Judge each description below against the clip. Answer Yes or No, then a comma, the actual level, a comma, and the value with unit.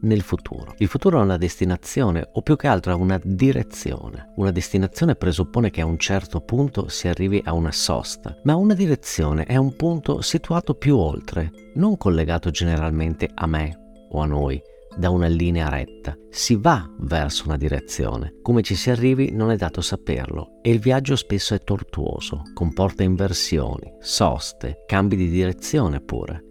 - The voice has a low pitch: Yes, very low, 95 Hz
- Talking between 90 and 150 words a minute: No, fast, 170 wpm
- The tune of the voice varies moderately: No, wide, 6.0 semitones